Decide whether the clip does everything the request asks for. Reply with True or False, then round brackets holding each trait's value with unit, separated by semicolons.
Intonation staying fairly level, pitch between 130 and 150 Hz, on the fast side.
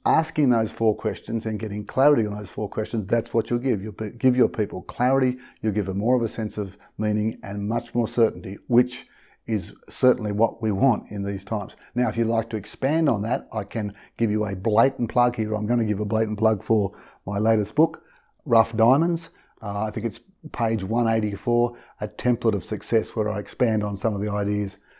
False (2.2 semitones; 110 Hz; 215 wpm)